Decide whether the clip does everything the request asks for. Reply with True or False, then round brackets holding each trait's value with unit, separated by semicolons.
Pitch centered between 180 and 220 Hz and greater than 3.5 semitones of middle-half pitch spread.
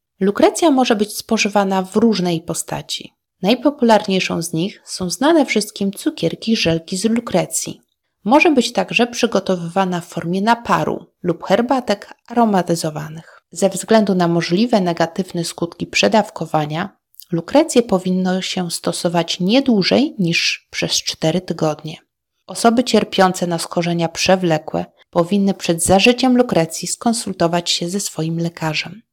True (190 Hz; 4.7 semitones)